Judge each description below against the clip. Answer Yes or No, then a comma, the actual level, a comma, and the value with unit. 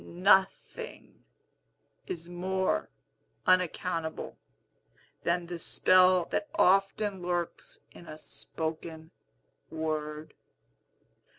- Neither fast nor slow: No, slow, 75 wpm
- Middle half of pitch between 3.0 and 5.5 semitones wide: No, narrow, 2.6 semitones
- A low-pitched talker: No, medium, 175 Hz